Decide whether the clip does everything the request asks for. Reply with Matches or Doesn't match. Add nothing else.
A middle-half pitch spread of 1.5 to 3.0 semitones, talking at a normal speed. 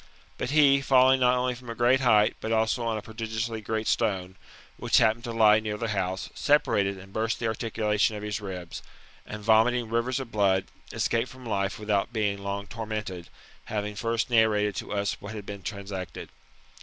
Matches